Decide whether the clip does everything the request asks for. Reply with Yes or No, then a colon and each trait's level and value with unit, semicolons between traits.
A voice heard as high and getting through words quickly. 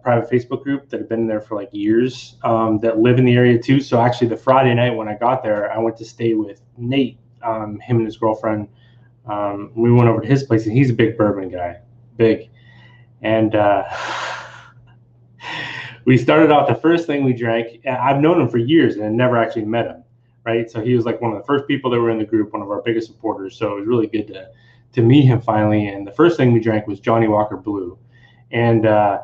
No: low, 115 Hz; fast, 235 wpm